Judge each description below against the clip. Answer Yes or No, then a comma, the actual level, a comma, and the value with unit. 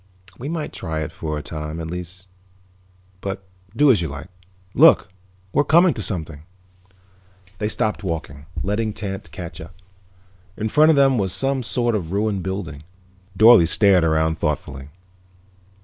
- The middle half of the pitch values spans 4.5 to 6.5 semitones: Yes, wide, 5.5 semitones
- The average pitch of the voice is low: Yes, very low, 95 Hz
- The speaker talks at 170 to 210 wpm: No, average, 155 wpm